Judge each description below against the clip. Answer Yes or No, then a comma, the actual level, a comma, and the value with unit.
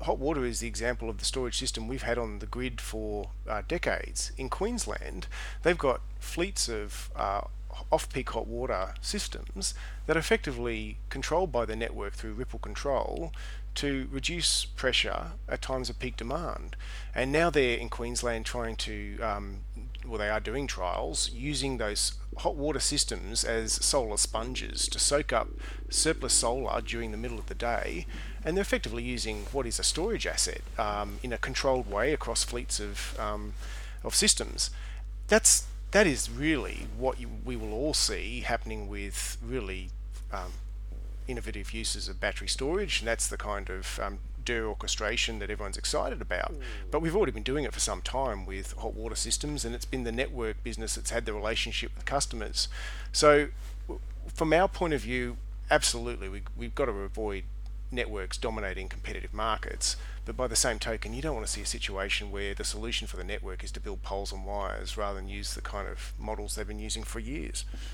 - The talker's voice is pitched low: Yes, low, 115 Hz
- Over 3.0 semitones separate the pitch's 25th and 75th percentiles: Yes, average, 3.4 semitones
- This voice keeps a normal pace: Yes, average, 185 wpm